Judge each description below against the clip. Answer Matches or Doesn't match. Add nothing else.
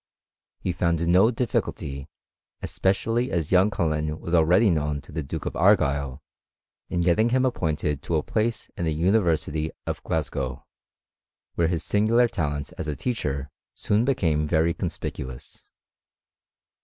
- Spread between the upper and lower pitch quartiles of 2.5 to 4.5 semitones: Doesn't match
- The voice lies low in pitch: Matches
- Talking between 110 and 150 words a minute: Matches